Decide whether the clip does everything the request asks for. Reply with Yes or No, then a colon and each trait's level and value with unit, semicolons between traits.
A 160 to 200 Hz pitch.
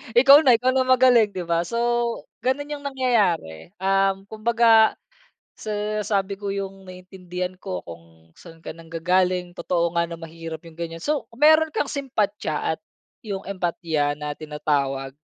Yes: high, 190 Hz